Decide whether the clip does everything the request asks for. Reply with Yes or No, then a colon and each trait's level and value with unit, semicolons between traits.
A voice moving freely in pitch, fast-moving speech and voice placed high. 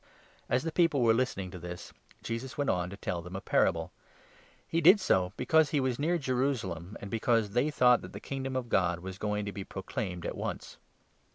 No: wide, 6.3 semitones; fast, 225 wpm; low, 115 Hz